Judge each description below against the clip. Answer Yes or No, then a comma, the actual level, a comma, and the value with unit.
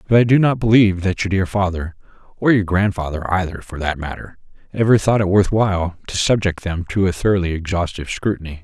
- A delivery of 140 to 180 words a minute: No, average, 190 wpm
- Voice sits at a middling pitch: No, very low, 95 Hz